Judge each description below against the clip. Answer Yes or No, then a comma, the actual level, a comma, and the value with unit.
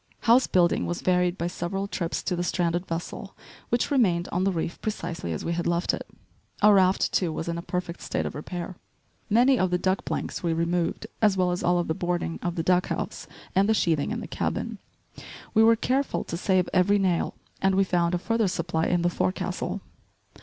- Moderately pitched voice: Yes, medium, 180 Hz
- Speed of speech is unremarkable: No, fast, 210 wpm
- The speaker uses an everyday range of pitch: No, narrow, 2.2 semitones